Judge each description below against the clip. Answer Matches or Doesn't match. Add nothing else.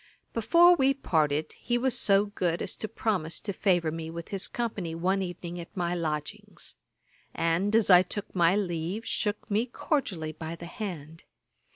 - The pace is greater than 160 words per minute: Matches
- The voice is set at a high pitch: Doesn't match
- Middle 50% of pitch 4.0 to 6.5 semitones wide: Matches